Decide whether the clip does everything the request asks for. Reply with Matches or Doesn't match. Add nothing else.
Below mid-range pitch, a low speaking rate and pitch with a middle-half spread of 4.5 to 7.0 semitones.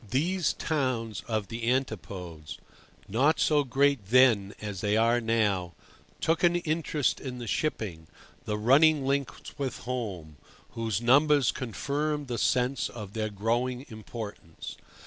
Matches